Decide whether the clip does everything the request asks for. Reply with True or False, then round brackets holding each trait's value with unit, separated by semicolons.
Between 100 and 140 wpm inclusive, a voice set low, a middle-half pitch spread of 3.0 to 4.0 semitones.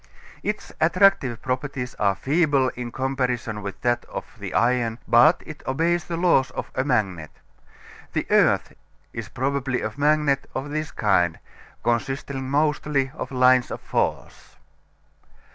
True (135 wpm; 130 Hz; 3.6 semitones)